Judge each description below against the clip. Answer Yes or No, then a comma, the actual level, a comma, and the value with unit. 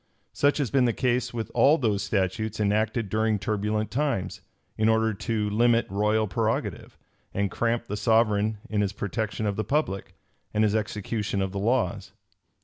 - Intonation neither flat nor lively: No, narrow, 2.2 semitones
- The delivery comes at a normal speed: Yes, average, 165 wpm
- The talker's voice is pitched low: Yes, low, 110 Hz